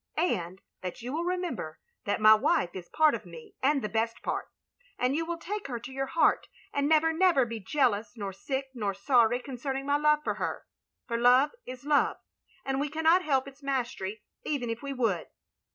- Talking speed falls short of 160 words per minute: No, average, 200 wpm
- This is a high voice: Yes, very high, 265 Hz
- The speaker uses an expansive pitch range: No, average, 4.8 semitones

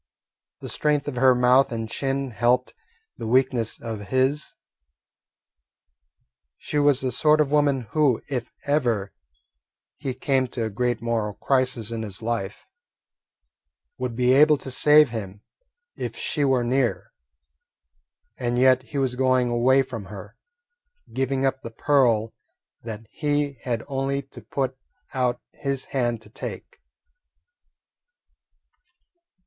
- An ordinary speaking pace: No, slow, 130 wpm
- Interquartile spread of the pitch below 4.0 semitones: Yes, average, 2.8 semitones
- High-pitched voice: No, low, 125 Hz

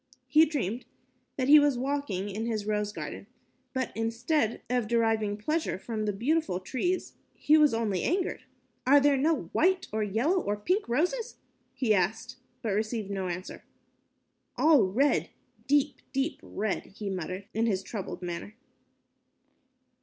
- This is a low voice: No, high, 230 Hz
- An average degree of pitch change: No, wide, 5.8 semitones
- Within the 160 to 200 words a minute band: No, average, 145 wpm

